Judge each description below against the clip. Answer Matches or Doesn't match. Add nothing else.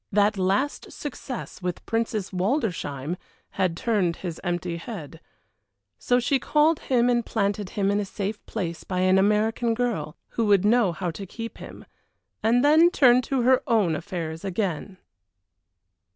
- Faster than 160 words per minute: Doesn't match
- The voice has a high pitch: Matches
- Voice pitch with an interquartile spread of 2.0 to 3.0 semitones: Doesn't match